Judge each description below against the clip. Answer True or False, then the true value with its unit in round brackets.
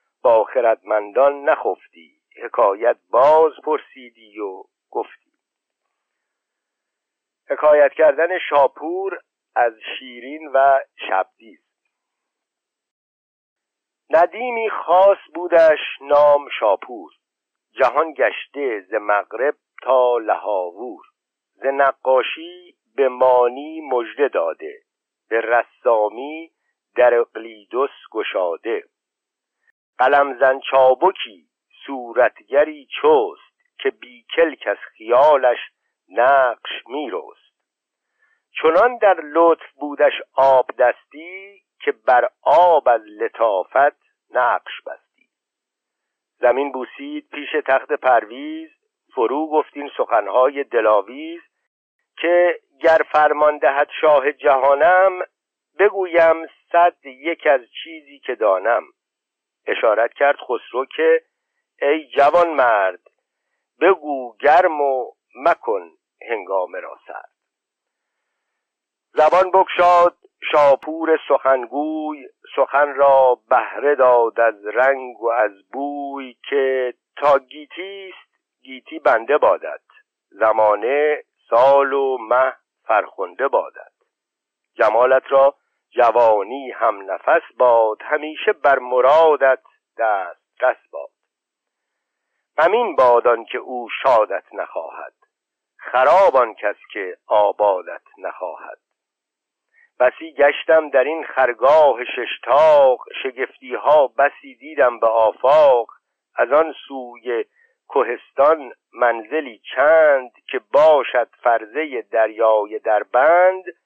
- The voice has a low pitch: False (160 Hz)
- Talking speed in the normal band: False (90 wpm)